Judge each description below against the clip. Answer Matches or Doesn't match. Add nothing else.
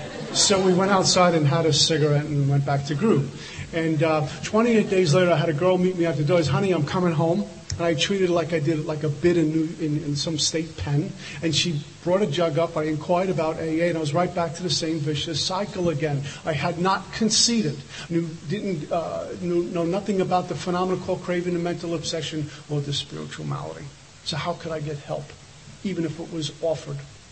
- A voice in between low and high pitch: Matches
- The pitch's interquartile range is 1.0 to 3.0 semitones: Matches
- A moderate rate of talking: Doesn't match